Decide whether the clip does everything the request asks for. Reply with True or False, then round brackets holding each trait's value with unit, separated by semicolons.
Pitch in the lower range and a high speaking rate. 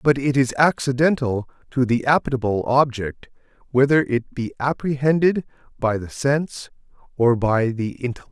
False (130 Hz; 135 wpm)